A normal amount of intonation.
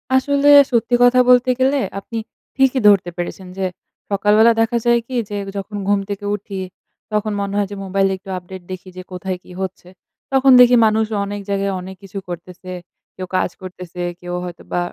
Yes: average, 4.0 semitones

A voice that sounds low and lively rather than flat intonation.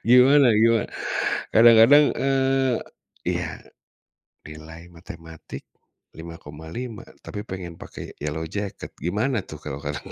Yes: low, 100 Hz; wide, 7.1 semitones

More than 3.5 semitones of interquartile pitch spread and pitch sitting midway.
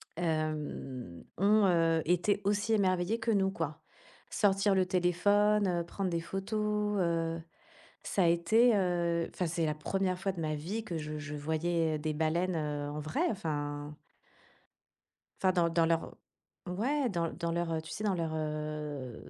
Yes: average, 3.9 semitones; medium, 170 Hz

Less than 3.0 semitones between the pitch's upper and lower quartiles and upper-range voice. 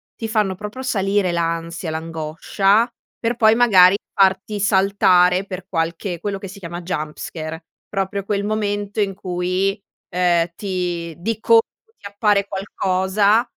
Yes: narrow, 2.6 semitones; high, 195 Hz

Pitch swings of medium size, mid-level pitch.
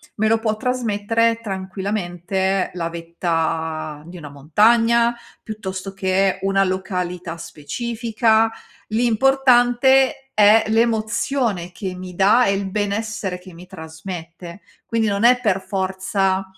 No: average, 3.9 semitones; high, 195 Hz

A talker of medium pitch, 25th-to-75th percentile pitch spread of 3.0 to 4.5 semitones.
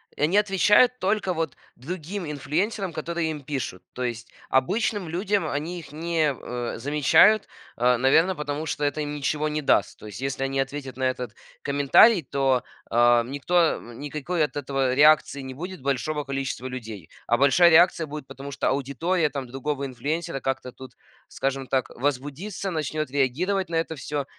Yes: medium, 145 Hz; average, 4.0 semitones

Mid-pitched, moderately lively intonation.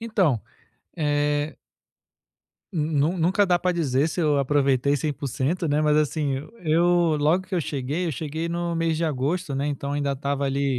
Yes: medium, 150 Hz; average, 3.1 semitones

